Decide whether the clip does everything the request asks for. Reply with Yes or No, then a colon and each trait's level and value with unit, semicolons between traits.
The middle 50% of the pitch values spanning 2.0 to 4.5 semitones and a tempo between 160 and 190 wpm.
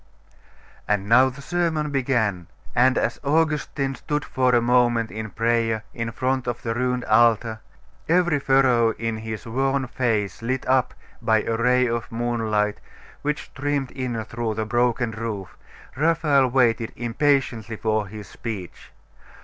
No: average, 3.0 semitones; average, 140 wpm